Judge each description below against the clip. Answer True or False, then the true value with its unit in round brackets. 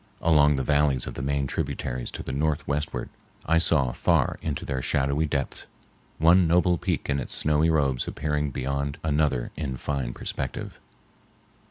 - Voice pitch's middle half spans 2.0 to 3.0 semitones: True (2.4 semitones)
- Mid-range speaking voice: False (70 Hz)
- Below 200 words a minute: True (155 wpm)